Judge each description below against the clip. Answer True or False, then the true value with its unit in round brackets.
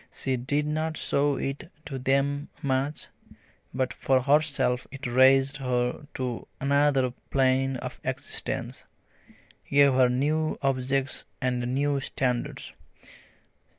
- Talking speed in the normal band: False (115 wpm)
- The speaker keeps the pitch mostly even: True (1.8 semitones)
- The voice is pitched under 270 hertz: True (135 Hz)